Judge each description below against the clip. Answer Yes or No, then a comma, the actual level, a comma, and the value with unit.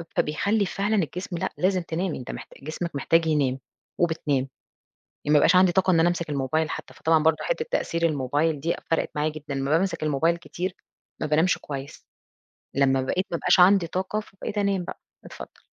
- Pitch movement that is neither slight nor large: Yes, average, 3.7 semitones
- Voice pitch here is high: No, medium, 165 Hz